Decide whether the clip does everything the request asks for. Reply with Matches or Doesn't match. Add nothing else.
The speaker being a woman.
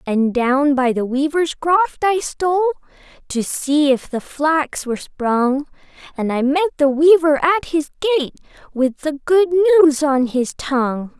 Matches